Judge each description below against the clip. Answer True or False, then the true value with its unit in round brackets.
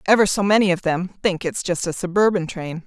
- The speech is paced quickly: True (230 wpm)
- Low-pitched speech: False (185 Hz)